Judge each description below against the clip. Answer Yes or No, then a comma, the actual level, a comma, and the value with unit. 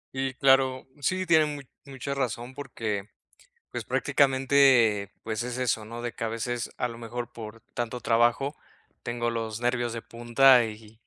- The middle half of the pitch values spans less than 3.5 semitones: Yes, average, 2.7 semitones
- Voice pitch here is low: Yes, low, 120 Hz